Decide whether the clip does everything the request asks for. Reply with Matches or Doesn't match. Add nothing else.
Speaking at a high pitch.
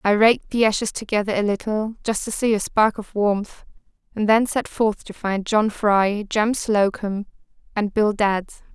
Matches